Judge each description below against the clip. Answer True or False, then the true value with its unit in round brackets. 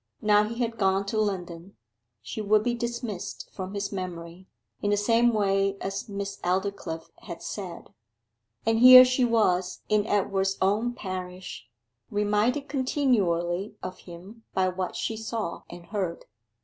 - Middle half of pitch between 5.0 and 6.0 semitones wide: False (3.2 semitones)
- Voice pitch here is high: True (200 Hz)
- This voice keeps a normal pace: True (145 wpm)